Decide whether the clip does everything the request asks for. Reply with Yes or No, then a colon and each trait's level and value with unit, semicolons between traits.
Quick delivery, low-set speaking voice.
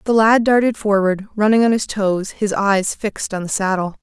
No: fast, 210 wpm; high, 205 Hz